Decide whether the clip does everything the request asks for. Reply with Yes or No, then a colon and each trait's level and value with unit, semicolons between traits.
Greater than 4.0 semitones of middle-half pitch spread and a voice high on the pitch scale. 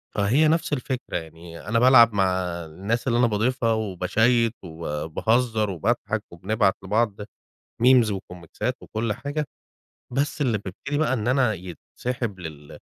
No: average, 5.2 semitones; low, 110 Hz